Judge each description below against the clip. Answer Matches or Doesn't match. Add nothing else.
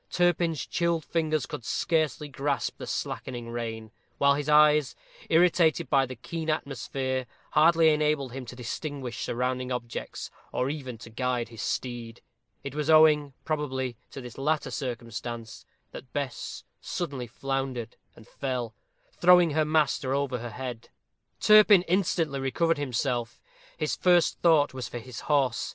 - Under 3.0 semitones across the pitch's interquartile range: Doesn't match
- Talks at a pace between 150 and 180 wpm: Doesn't match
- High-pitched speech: Doesn't match